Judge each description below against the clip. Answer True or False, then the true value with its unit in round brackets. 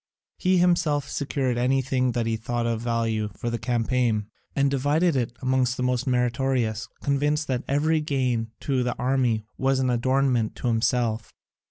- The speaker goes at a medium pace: True (160 wpm)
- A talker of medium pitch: False (125 Hz)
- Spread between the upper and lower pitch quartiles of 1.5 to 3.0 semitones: True (2.7 semitones)